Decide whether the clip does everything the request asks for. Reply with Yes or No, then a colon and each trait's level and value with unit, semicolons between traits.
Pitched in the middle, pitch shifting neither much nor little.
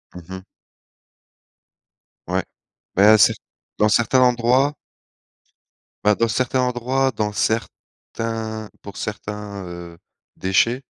No: low, 110 Hz; average, 3.1 semitones